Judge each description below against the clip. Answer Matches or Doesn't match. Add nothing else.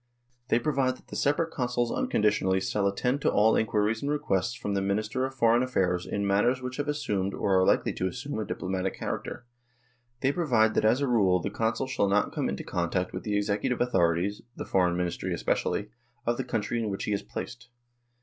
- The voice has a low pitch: Matches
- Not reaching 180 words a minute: Doesn't match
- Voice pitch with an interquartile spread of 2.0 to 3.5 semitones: Doesn't match